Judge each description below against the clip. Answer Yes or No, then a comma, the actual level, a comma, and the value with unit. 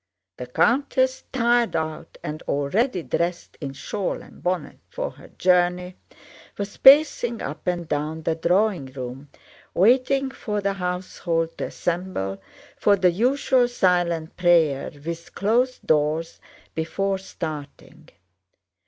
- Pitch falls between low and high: Yes, medium, 180 Hz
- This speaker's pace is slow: Yes, slow, 120 wpm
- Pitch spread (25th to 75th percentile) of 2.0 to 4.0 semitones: No, average, 5.1 semitones